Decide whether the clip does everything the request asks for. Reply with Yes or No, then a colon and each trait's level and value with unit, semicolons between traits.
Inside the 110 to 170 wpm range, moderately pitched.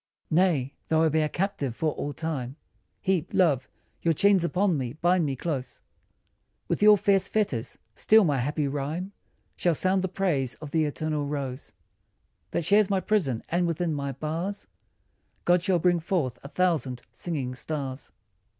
Yes: average, 160 wpm; medium, 160 Hz